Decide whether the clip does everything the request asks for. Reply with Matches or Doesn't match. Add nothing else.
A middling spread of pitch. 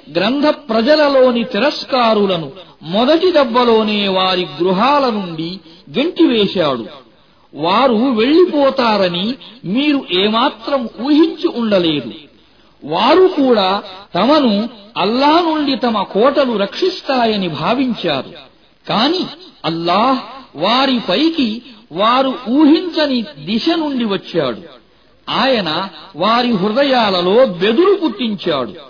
Doesn't match